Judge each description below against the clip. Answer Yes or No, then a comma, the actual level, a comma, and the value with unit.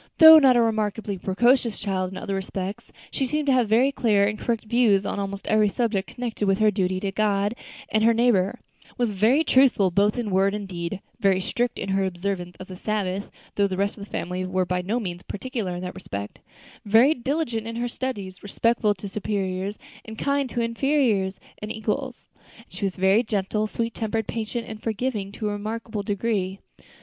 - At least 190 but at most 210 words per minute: Yes, average, 195 wpm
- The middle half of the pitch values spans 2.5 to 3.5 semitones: Yes, average, 3.2 semitones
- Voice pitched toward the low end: No, high, 210 Hz